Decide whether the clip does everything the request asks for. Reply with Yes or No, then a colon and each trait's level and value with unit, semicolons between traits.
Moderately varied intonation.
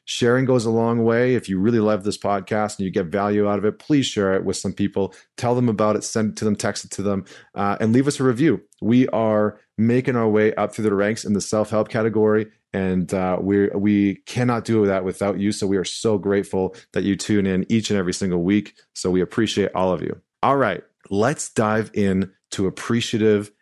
No: narrow, 2.1 semitones